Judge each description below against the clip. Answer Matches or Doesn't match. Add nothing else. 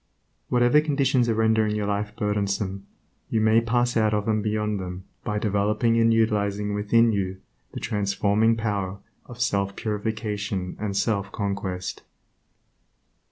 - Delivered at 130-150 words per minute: Matches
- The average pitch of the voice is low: Matches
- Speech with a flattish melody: Matches